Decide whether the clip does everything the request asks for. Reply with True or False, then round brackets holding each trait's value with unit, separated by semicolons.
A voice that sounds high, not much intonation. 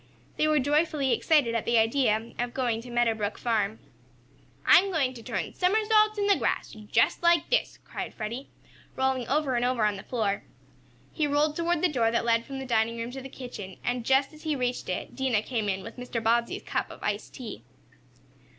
False (250 Hz; 4.5 semitones)